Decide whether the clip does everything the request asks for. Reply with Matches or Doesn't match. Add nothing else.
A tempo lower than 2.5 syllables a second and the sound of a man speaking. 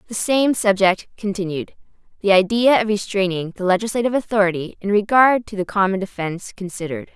Doesn't match